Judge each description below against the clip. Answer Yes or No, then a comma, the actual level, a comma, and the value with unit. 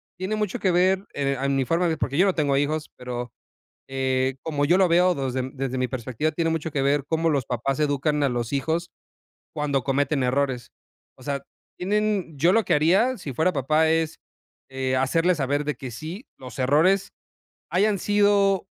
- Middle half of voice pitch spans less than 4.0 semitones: No, average, 4.8 semitones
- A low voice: No, medium, 150 Hz